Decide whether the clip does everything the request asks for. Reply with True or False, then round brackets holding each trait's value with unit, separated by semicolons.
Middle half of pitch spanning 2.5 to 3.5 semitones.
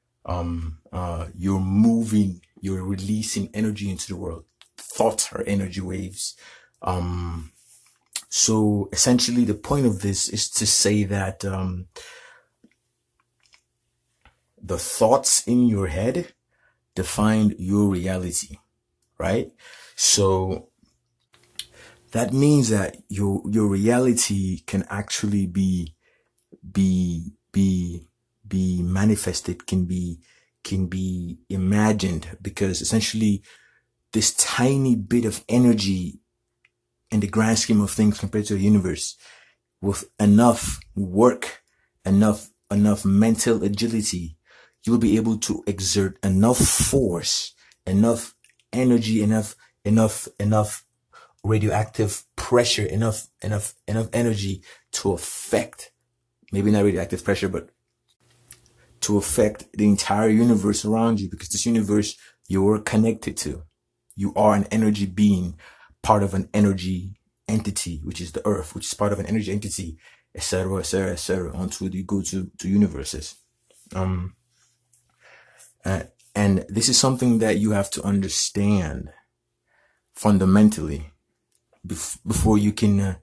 True (2.8 semitones)